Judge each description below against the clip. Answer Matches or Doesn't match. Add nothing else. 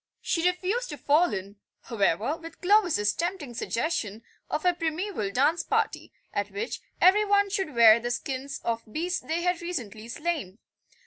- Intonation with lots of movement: Matches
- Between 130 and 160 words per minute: Matches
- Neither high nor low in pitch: Doesn't match